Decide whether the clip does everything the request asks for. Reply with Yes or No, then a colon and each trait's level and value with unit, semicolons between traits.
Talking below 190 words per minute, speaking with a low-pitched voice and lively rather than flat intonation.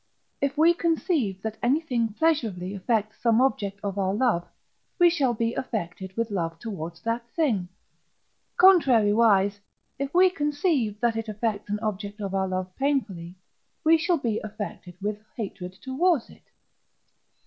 No: average, 145 wpm; high, 225 Hz; wide, 5.8 semitones